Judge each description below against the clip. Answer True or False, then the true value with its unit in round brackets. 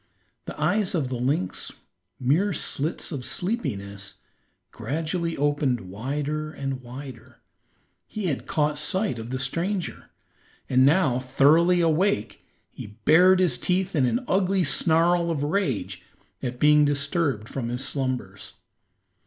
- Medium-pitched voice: True (145 Hz)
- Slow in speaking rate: True (130 wpm)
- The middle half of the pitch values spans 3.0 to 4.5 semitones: False (5.1 semitones)